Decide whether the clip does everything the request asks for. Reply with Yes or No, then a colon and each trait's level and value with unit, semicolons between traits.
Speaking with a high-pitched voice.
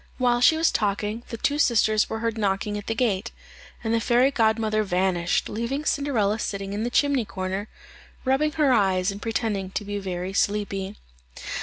Yes: high, 215 Hz